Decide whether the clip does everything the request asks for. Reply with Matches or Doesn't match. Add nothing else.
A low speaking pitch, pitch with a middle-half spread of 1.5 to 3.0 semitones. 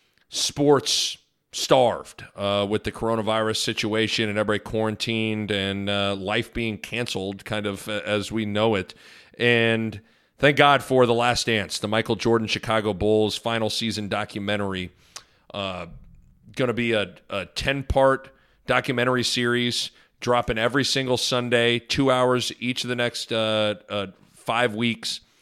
Matches